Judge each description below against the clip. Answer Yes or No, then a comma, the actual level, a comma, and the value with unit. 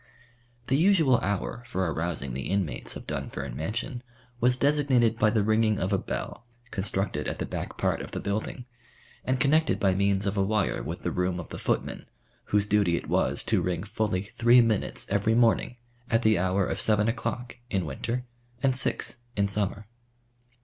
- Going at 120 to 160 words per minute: No, average, 180 wpm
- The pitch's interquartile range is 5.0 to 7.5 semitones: No, average, 4.0 semitones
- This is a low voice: Yes, low, 105 Hz